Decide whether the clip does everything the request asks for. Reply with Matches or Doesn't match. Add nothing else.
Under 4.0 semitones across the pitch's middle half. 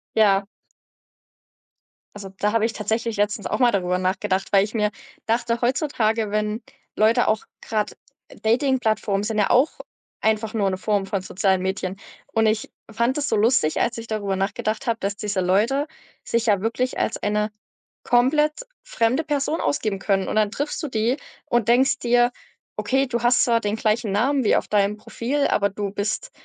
Matches